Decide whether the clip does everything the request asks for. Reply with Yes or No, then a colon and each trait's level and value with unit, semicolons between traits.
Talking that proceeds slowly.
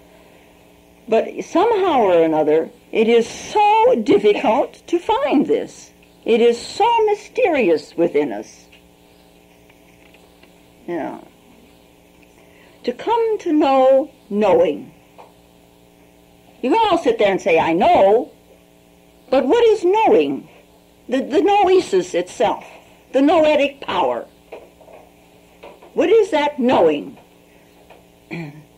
Yes: slow, 100 wpm